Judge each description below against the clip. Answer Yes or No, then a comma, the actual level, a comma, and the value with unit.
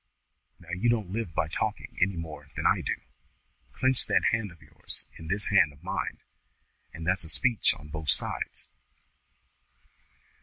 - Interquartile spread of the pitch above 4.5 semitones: Yes, average, 4.9 semitones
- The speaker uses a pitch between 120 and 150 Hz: No, very low, 90 Hz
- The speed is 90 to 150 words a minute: No, average, 160 wpm